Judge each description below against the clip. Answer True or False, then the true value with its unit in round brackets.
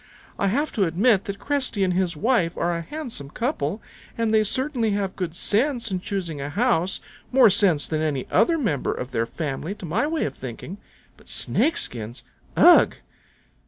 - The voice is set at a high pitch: True (195 Hz)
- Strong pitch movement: True (6.6 semitones)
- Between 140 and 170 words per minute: False (180 wpm)